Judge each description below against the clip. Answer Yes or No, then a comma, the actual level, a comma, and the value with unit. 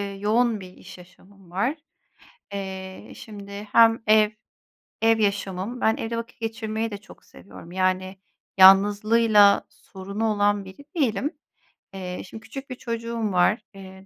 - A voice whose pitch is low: No, high, 205 Hz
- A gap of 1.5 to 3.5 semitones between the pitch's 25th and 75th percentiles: Yes, average, 2.8 semitones